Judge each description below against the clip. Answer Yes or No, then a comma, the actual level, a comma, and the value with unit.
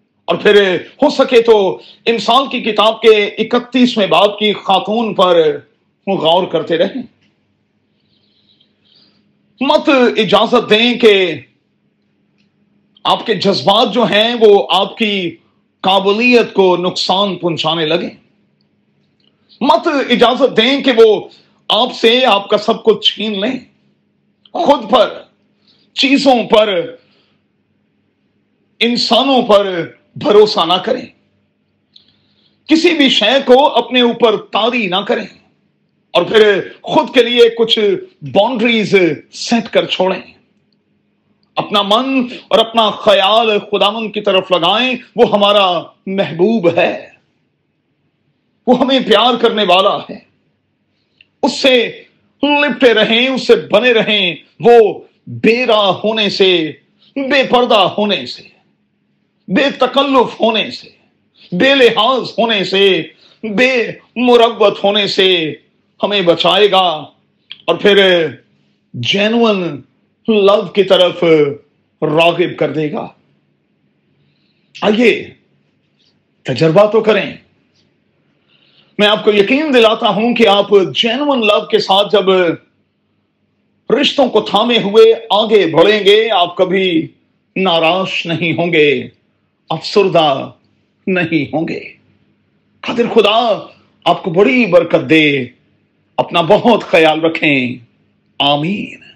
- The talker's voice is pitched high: Yes, high, 210 Hz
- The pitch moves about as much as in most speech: Yes, average, 4.5 semitones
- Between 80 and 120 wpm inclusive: Yes, slow, 110 wpm